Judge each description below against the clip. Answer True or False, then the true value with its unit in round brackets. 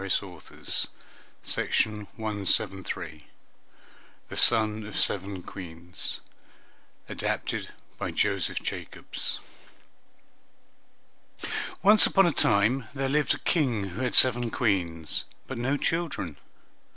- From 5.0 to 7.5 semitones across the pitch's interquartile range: True (5.5 semitones)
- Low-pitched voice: True (105 Hz)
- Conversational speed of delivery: False (95 wpm)